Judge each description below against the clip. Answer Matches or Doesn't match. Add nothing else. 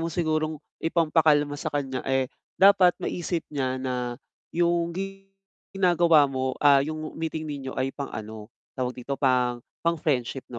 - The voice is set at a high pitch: Doesn't match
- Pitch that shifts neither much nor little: Matches